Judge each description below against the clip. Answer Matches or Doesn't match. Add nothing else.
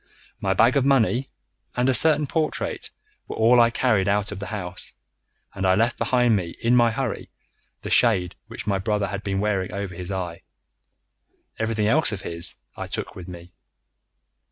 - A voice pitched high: Doesn't match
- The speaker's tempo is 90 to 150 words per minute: Doesn't match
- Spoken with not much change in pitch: Doesn't match